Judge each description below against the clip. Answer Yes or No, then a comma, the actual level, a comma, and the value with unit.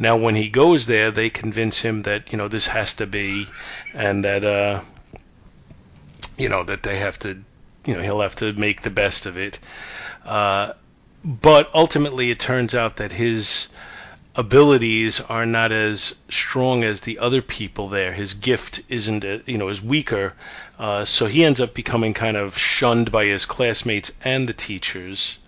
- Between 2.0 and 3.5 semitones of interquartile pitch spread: Yes, average, 3.1 semitones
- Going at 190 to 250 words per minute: No, average, 175 wpm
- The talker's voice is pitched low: Yes, low, 110 Hz